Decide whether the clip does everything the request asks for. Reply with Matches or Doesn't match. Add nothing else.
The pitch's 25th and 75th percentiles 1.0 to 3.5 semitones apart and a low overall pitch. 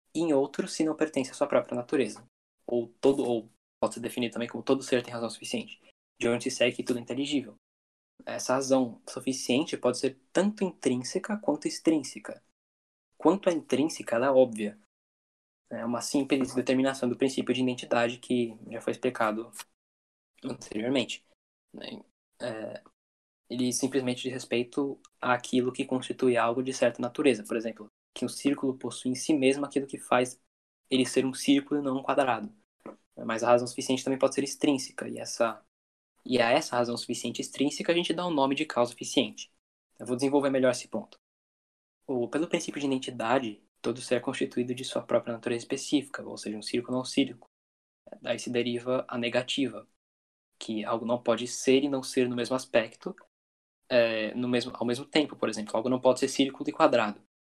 Matches